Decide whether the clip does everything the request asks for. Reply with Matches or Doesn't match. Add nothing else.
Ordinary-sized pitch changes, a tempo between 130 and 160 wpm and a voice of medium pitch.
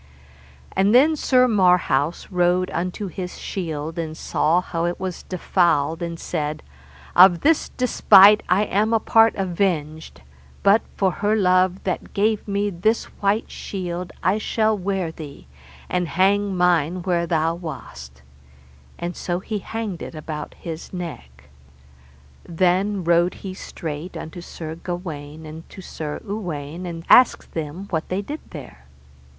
Matches